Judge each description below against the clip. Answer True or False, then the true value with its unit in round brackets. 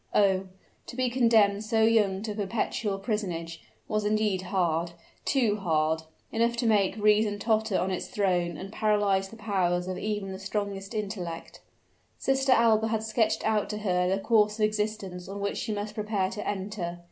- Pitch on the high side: True (205 Hz)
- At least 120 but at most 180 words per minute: True (170 wpm)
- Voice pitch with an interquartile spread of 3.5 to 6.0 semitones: False (2.4 semitones)